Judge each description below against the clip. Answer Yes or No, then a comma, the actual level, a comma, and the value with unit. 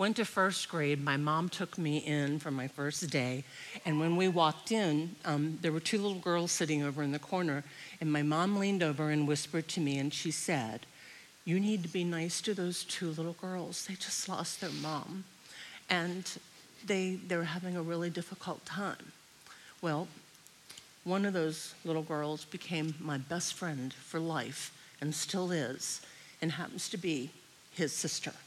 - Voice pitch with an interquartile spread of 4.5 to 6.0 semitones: No, average, 3.4 semitones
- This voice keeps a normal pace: Yes, average, 180 wpm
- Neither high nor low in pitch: Yes, medium, 165 Hz